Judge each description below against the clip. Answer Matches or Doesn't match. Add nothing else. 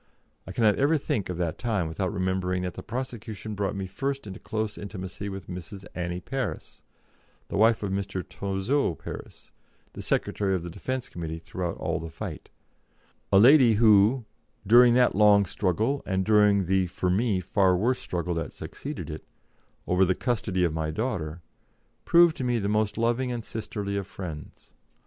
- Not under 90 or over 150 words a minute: Doesn't match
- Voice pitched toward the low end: Matches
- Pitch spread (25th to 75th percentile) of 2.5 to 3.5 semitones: Doesn't match